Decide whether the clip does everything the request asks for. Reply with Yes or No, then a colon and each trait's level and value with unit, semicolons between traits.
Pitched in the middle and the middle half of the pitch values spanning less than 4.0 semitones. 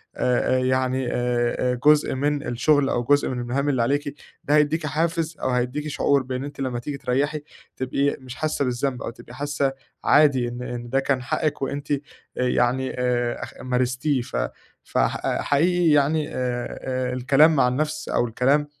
No: low, 130 Hz; average, 2.7 semitones